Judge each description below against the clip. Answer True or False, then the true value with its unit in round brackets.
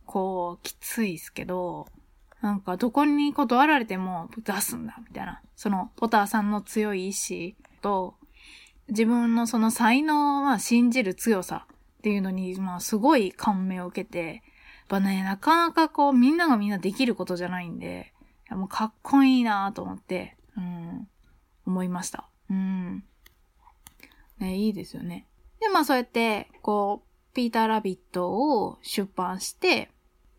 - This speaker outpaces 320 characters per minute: False (300 characters per minute)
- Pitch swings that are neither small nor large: True (4.7 semitones)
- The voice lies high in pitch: True (210 Hz)